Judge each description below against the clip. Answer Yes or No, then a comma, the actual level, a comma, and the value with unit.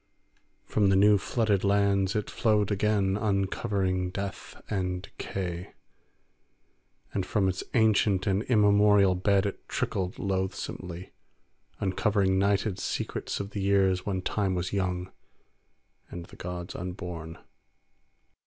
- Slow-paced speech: Yes, slow, 115 wpm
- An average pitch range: No, narrow, 1.8 semitones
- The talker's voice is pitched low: Yes, very low, 95 Hz